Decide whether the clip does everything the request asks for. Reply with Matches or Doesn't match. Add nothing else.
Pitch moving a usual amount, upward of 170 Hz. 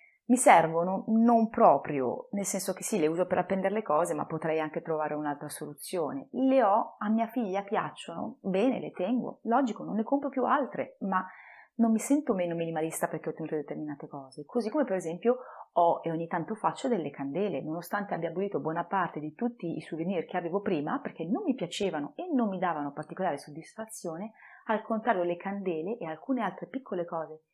Doesn't match